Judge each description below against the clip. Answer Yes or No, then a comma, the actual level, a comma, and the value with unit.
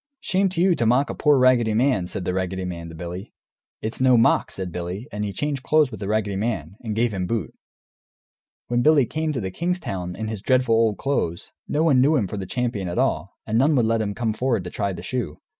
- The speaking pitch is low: Yes, low, 115 Hz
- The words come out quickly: Yes, fast, 245 wpm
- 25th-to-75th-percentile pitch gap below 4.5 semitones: No, average, 5.3 semitones